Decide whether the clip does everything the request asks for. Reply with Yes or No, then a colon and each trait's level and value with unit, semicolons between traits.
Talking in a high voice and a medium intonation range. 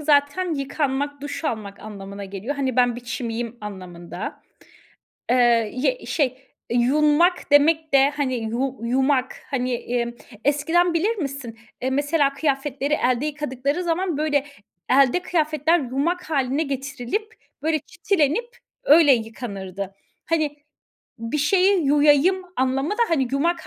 Yes: very high, 280 Hz; average, 4.0 semitones